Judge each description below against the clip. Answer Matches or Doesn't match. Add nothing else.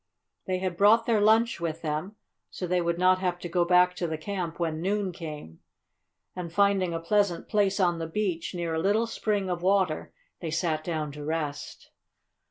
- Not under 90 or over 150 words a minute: Doesn't match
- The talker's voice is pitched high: Doesn't match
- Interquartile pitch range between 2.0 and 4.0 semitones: Matches